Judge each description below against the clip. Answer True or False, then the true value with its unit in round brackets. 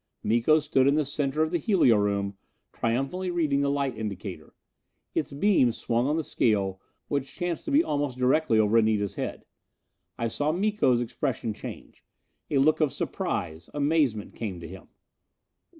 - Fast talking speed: False (160 wpm)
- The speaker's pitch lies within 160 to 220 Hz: False (135 Hz)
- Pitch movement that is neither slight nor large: False (5.9 semitones)